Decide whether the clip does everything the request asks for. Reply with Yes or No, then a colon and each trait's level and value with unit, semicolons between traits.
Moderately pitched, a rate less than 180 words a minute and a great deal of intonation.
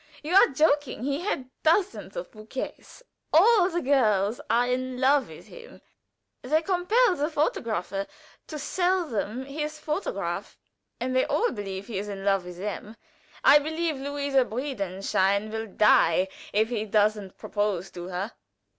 No: very high, 255 Hz; average, 150 wpm; wide, 6.9 semitones